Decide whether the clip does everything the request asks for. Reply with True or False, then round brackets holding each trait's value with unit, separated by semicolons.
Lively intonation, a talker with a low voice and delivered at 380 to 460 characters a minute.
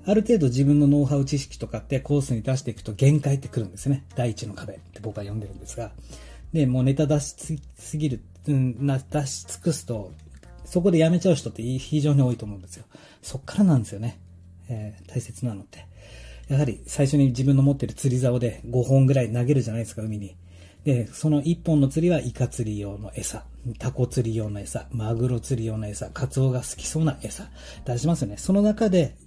False (4.8 semitones; 125 Hz; 395 characters per minute)